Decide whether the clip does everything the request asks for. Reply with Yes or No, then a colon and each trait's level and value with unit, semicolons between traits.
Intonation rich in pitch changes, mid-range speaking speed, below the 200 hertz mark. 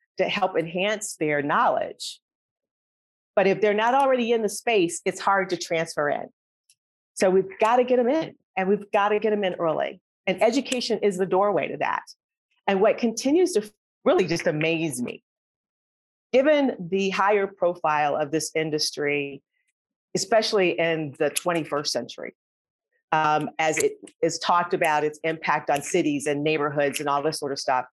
Yes: wide, 5.7 semitones; average, 170 wpm; medium, 185 Hz